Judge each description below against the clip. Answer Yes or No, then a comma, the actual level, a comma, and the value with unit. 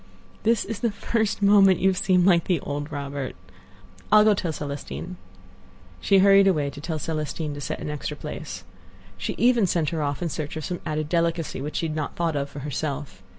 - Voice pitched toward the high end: No, medium, 165 Hz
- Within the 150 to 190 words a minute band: No, fast, 205 wpm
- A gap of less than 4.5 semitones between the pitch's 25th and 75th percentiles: No, average, 4.8 semitones